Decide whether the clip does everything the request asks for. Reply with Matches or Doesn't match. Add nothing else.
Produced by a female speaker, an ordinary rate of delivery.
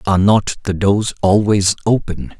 Doesn't match